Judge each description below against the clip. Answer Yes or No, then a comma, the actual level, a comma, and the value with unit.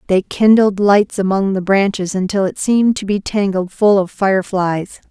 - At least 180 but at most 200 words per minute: Yes, average, 190 wpm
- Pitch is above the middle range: Yes, high, 195 Hz